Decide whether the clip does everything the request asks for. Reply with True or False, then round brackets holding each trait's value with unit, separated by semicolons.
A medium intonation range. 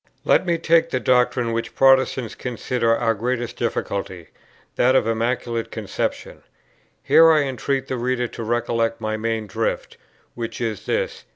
False (2.1 semitones)